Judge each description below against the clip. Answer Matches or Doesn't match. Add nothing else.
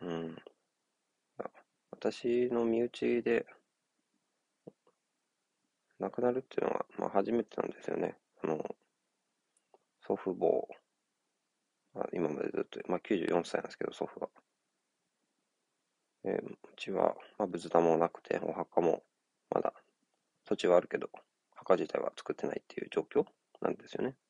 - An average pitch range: Doesn't match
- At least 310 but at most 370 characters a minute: Doesn't match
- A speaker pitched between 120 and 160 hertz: Doesn't match